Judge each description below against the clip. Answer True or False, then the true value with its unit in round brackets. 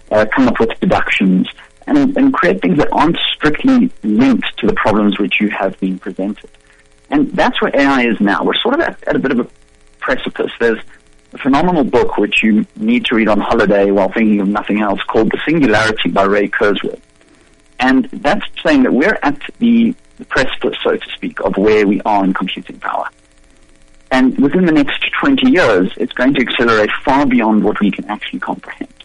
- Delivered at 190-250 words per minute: True (195 wpm)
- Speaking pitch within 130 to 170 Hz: False (105 Hz)